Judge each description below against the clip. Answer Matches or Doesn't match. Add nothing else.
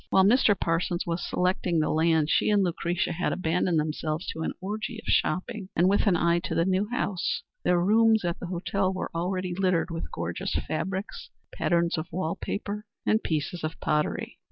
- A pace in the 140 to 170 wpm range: Doesn't match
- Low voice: Doesn't match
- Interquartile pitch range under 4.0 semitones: Matches